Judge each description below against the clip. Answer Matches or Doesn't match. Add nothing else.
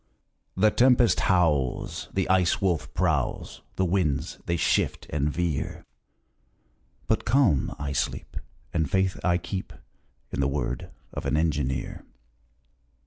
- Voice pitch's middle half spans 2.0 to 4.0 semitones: Doesn't match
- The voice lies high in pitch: Doesn't match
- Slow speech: Matches